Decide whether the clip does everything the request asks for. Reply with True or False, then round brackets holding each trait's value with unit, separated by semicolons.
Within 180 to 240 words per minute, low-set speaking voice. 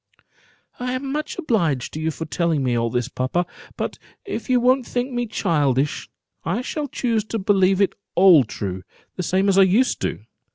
False (195 wpm; 190 Hz)